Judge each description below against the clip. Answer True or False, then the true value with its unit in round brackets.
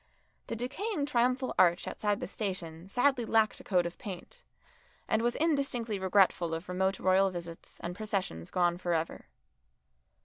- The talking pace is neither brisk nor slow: True (150 wpm)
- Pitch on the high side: True (195 Hz)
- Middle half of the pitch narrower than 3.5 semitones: False (5.1 semitones)